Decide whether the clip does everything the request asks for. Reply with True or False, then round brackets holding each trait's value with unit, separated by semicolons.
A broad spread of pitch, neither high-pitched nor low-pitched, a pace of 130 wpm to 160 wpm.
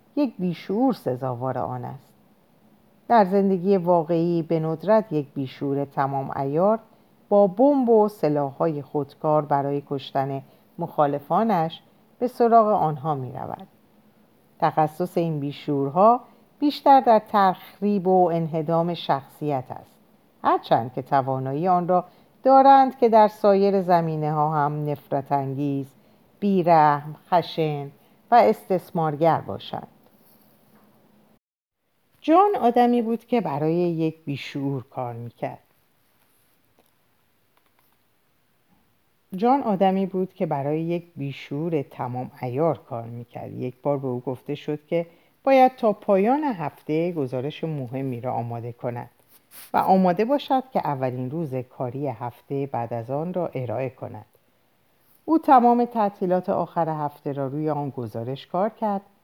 False (6.4 semitones; 160 Hz; 120 wpm)